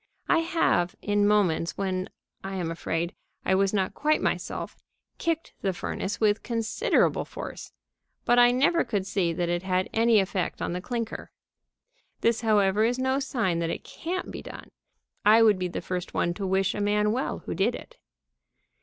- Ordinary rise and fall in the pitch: Yes, average, 4.1 semitones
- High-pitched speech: Yes, high, 205 Hz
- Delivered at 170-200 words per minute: Yes, average, 180 wpm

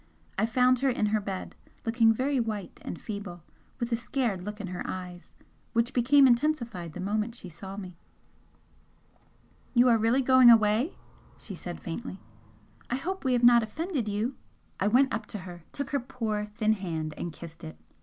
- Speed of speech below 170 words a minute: No, average, 180 wpm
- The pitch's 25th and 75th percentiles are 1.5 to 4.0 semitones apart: No, average, 4.6 semitones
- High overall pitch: Yes, high, 220 Hz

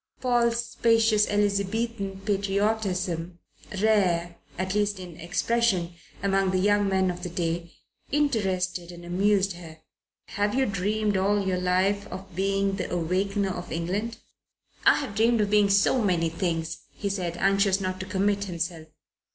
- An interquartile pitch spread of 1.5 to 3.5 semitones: Yes, narrow, 2.4 semitones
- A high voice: Yes, high, 195 Hz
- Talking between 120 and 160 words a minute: Yes, average, 145 wpm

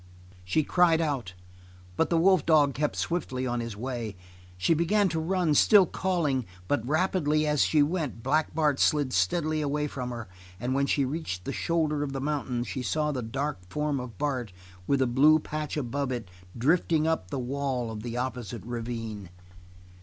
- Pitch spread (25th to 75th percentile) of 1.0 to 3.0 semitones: No, average, 4.2 semitones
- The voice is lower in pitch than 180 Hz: Yes, medium, 140 Hz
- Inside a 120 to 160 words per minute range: No, average, 180 wpm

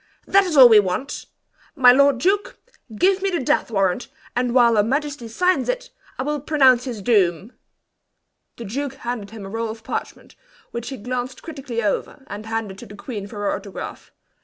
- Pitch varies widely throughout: No, average, 4.7 semitones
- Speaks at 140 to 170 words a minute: No, average, 185 wpm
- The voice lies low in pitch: No, high, 245 Hz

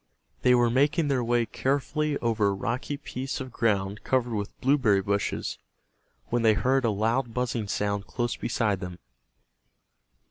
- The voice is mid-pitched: No, low, 120 Hz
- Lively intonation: No, average, 4.0 semitones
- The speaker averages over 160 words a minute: No, average, 150 wpm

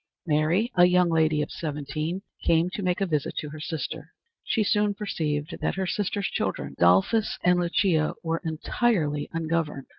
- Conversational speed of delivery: Yes, average, 160 wpm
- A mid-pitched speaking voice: Yes, medium, 165 Hz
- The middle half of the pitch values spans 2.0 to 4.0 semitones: Yes, average, 3.5 semitones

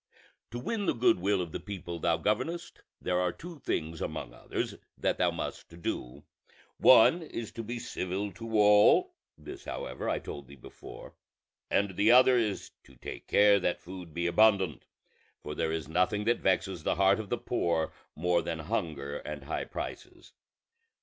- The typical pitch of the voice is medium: No, very low, 95 Hz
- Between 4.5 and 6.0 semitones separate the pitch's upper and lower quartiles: Yes, average, 4.8 semitones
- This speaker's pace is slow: No, average, 170 wpm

